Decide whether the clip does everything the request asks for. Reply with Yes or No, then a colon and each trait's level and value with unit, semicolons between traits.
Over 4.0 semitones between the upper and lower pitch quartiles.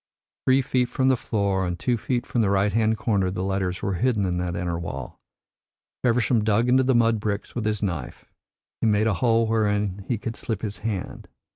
No: average, 3.2 semitones